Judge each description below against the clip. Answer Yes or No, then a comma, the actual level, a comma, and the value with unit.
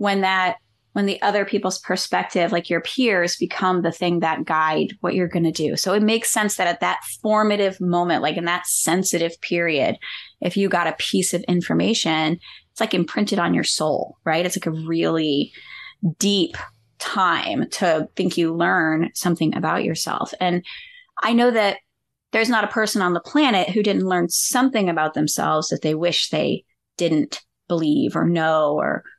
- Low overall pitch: No, medium, 175 Hz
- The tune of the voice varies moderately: Yes, average, 3.7 semitones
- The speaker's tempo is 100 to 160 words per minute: No, average, 175 wpm